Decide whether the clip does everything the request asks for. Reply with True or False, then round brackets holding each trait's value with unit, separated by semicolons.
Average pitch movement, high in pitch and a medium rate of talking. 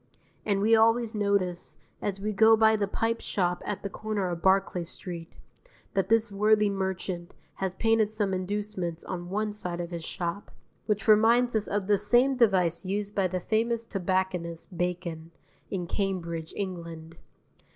True (3.2 semitones; 195 Hz; 160 wpm)